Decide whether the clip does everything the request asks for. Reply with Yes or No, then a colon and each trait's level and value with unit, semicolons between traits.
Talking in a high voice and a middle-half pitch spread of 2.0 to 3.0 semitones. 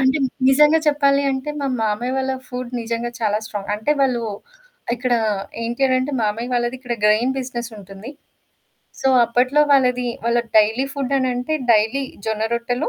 Yes: high, 245 Hz; narrow, 2.5 semitones